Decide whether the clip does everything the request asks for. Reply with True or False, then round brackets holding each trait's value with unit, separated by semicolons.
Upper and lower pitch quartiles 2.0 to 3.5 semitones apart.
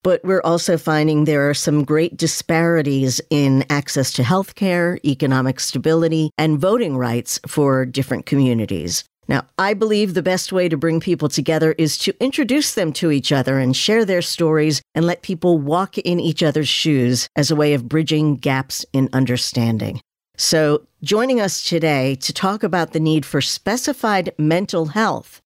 False (4.1 semitones)